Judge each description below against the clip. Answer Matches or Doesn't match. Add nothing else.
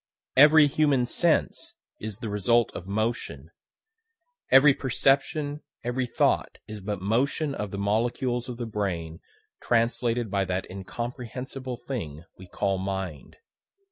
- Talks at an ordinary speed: Doesn't match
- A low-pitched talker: Matches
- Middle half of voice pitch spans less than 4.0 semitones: Doesn't match